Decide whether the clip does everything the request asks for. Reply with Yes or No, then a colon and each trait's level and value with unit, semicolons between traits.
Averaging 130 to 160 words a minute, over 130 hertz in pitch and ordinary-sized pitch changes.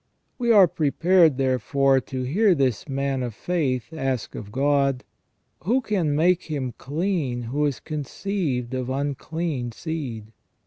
Yes: average, 140 wpm; medium, 140 Hz; average, 4.3 semitones